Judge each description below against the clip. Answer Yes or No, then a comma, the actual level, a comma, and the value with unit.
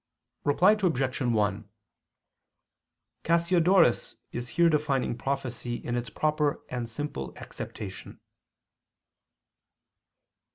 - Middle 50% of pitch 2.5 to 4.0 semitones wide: No, average, 5.2 semitones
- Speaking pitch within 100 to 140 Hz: Yes, low, 135 Hz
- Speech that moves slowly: Yes, slow, 80 wpm